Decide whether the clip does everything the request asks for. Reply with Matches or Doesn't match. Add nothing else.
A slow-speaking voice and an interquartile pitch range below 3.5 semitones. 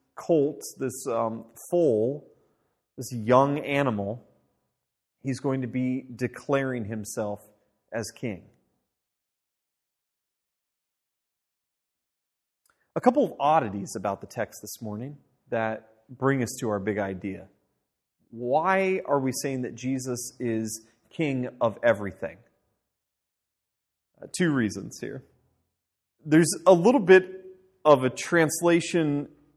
Doesn't match